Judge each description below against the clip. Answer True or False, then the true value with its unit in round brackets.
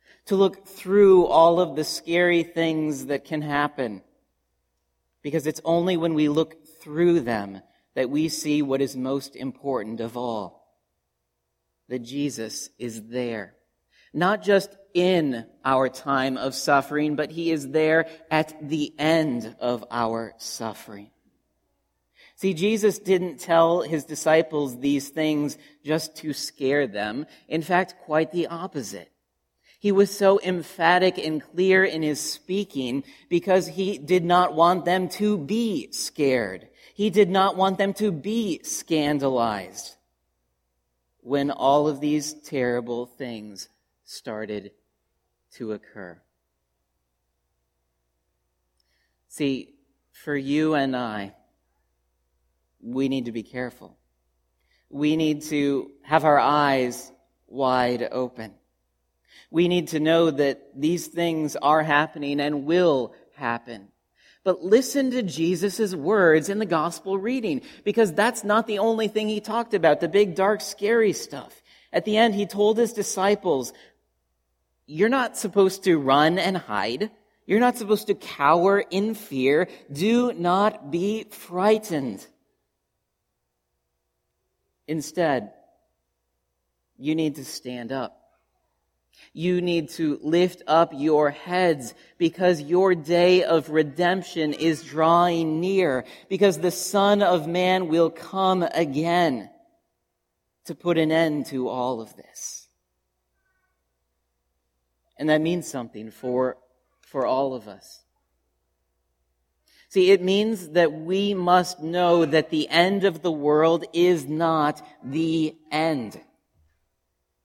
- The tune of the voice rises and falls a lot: True (8.0 semitones)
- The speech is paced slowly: True (125 wpm)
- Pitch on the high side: False (150 Hz)